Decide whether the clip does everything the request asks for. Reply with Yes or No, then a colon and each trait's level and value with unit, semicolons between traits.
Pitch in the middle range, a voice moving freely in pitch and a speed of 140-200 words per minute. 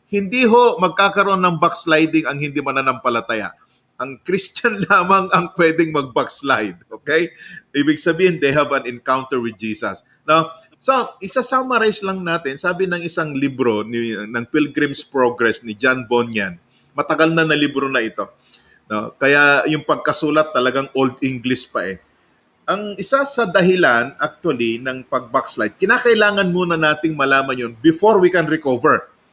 Yes: medium, 155 Hz; wide, 5.9 semitones; average, 145 wpm